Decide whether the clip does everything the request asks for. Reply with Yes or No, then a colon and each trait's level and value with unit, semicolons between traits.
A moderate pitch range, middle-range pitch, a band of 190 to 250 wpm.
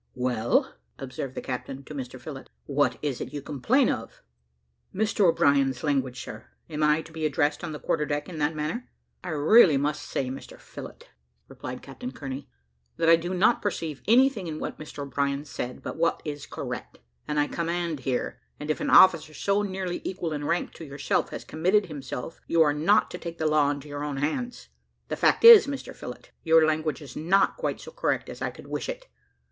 Yes: average, 3.8 semitones; medium, 155 Hz; average, 200 wpm